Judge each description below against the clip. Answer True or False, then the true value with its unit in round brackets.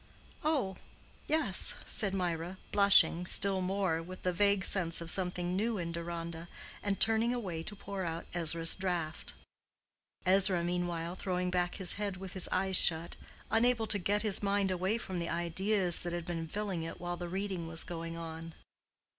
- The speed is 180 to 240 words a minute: False (170 wpm)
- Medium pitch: True (180 Hz)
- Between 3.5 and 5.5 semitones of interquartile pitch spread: False (2.8 semitones)